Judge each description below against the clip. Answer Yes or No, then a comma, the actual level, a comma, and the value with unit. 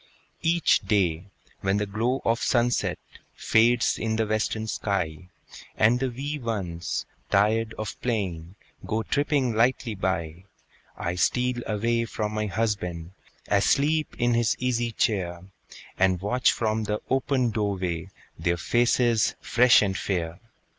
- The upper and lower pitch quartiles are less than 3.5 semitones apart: No, average, 4.0 semitones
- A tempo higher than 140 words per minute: No, slow, 135 wpm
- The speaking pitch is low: Yes, low, 110 Hz